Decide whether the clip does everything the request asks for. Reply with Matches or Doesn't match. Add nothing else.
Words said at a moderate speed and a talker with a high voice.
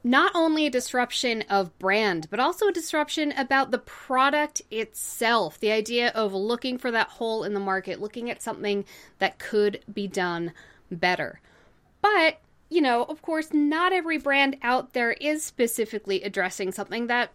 Matches